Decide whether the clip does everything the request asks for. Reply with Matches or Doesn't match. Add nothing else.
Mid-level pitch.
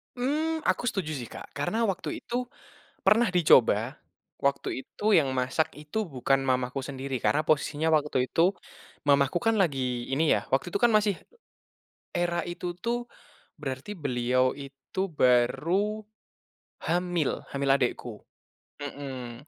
Matches